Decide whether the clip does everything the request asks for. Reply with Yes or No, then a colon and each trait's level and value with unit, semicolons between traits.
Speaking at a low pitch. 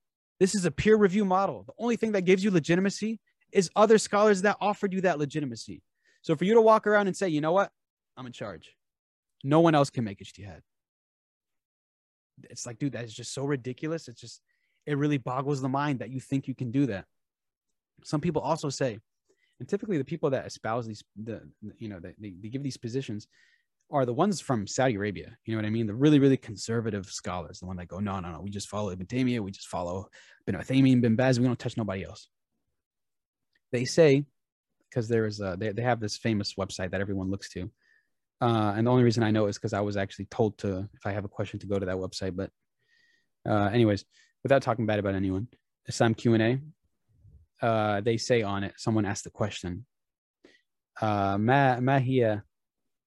Yes: low, 120 Hz